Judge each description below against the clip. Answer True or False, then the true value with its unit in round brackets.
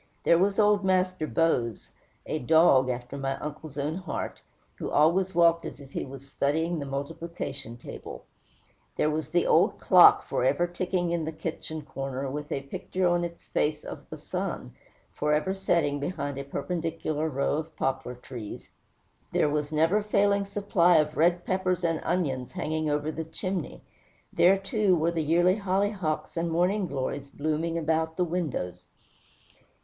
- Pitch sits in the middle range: True (160 Hz)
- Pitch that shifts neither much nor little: True (3.7 semitones)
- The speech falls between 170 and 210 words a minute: False (160 wpm)